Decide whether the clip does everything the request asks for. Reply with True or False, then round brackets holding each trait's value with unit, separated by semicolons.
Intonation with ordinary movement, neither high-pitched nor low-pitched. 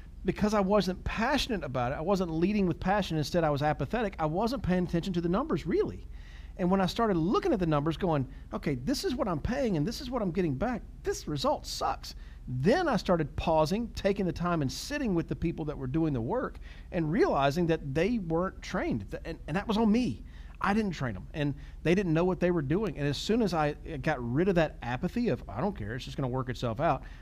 True (4.8 semitones; 170 Hz)